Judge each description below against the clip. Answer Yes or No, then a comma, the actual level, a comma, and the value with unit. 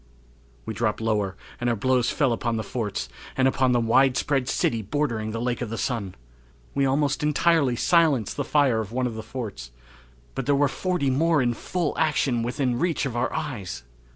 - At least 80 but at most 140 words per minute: No, average, 190 wpm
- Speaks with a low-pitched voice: Yes, low, 125 Hz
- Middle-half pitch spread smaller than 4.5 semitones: Yes, average, 3.9 semitones